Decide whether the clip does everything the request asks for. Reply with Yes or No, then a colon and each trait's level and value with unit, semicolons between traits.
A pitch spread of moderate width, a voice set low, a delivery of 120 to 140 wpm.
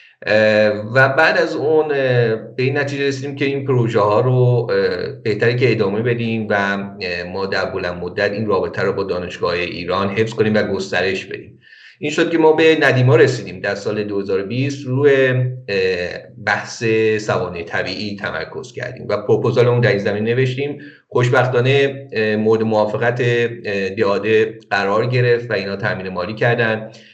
No: average, 4.4 semitones; low, 115 Hz; average, 150 wpm